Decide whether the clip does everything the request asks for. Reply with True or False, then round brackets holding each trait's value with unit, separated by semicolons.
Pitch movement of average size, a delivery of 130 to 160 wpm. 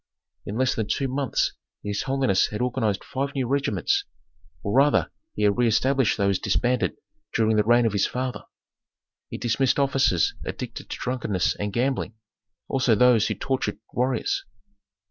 True (3.9 semitones; 150 wpm)